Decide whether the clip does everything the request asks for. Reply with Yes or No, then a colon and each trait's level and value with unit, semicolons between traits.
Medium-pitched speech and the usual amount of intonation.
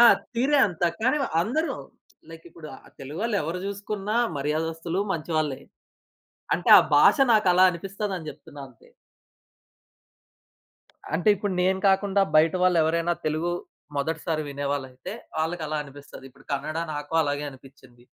Yes: medium, 165 Hz; average, 4.6 semitones